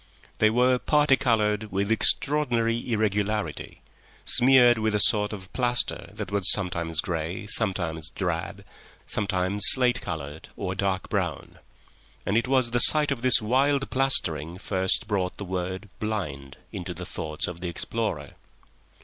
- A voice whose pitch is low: Yes, low, 105 Hz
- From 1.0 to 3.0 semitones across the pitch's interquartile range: No, average, 5.2 semitones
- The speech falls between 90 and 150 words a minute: Yes, average, 140 wpm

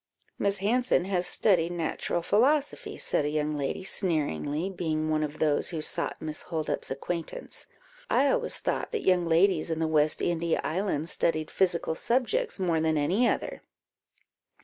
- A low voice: No, medium, 170 Hz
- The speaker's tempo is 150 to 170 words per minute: Yes, average, 155 wpm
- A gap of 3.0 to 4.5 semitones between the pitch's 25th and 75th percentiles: Yes, average, 3.7 semitones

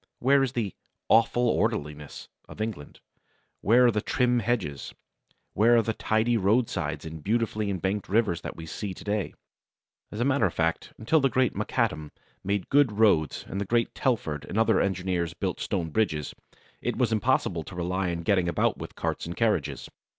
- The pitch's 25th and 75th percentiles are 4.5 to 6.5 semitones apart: Yes, average, 5.2 semitones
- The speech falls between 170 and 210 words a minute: Yes, average, 180 wpm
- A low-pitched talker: Yes, low, 105 Hz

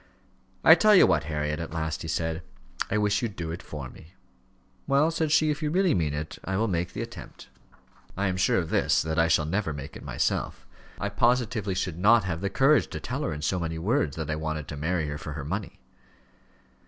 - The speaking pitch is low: Yes, very low, 85 Hz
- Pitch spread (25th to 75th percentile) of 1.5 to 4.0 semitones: No, wide, 5.5 semitones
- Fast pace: Yes, fast, 230 wpm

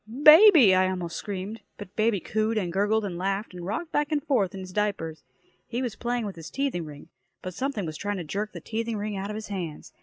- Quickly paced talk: Yes, fast, 235 wpm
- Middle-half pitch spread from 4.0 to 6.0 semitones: No, average, 3.6 semitones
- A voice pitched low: No, high, 205 Hz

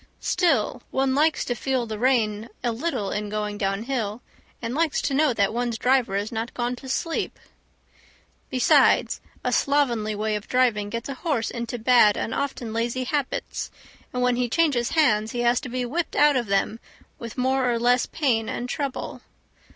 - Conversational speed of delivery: Yes, average, 180 wpm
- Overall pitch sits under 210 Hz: No, high, 245 Hz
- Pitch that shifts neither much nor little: Yes, average, 3.2 semitones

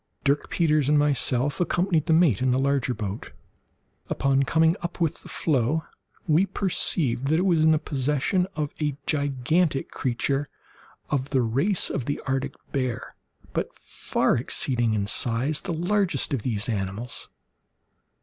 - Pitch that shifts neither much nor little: Yes, average, 4.1 semitones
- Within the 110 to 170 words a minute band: Yes, average, 150 wpm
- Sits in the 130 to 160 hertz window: Yes, medium, 140 Hz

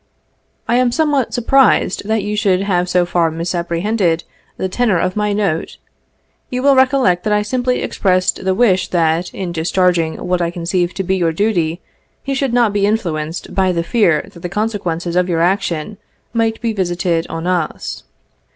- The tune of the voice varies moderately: Yes, average, 4.0 semitones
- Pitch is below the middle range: No, medium, 185 Hz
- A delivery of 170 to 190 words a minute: Yes, average, 180 wpm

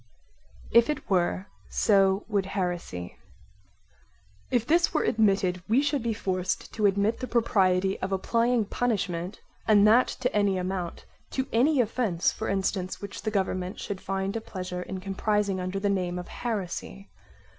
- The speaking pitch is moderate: No, high, 195 Hz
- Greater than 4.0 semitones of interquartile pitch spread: No, average, 3.4 semitones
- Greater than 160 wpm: No, average, 155 wpm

